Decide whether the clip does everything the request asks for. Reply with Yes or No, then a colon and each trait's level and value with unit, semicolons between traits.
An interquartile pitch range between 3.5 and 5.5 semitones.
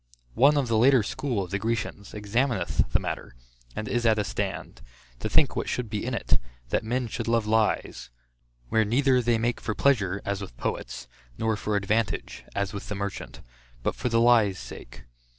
No: average, 3.0 semitones